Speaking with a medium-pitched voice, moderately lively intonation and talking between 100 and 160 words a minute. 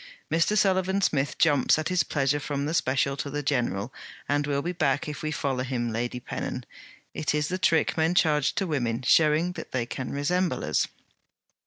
No: medium, 145 Hz; average, 3.5 semitones; average, 190 wpm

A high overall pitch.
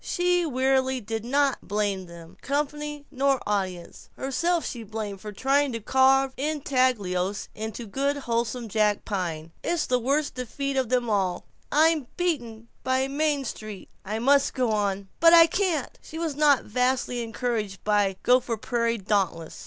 Yes: very high, 250 Hz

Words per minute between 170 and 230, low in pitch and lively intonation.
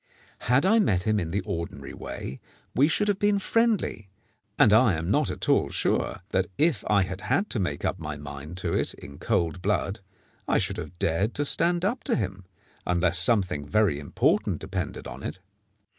Yes: average, 190 wpm; low, 100 Hz; wide, 8.8 semitones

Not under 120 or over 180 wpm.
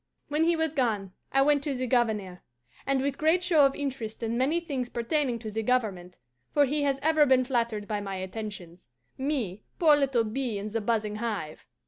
No: average, 195 wpm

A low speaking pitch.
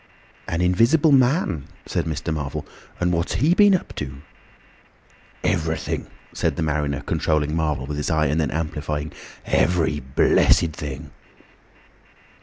Yes: very low, 80 Hz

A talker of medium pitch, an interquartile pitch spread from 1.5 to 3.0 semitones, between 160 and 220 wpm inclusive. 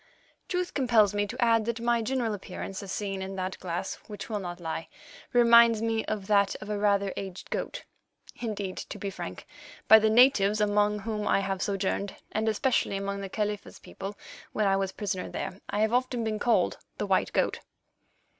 No: high, 210 Hz; narrow, 2.5 semitones; average, 190 wpm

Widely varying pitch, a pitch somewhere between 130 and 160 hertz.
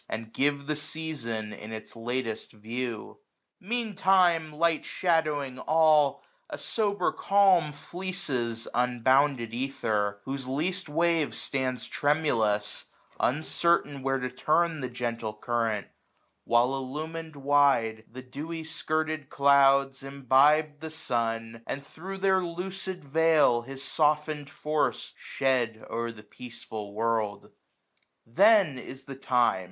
No: average, 4.9 semitones; medium, 140 Hz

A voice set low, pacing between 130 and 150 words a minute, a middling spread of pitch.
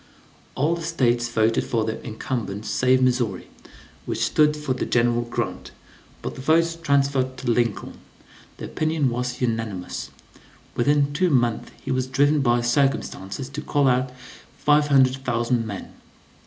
Yes: low, 130 Hz; average, 140 wpm; average, 3.2 semitones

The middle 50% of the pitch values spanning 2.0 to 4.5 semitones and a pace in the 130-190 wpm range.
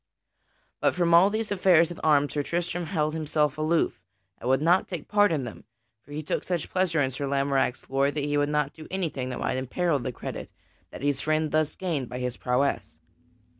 No: average, 3.6 semitones; fast, 205 wpm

